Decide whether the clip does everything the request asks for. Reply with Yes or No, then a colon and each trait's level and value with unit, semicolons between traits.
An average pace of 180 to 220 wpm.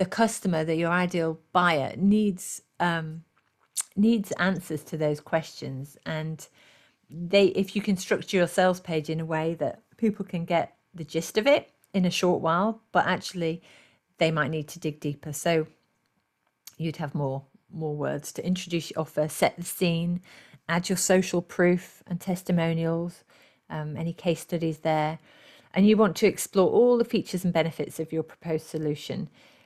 No: average, 170 wpm